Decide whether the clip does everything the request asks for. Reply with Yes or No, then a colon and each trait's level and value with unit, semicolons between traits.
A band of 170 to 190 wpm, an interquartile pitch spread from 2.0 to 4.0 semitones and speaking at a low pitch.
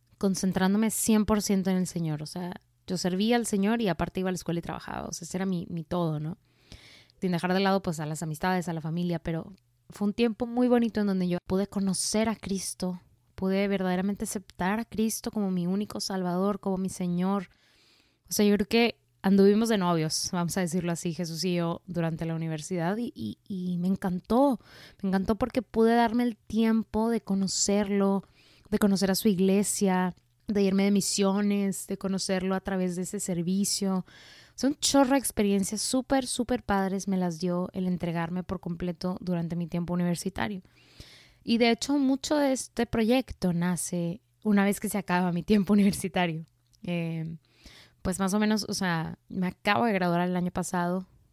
No: average, 185 wpm; average, 2.9 semitones; high, 190 Hz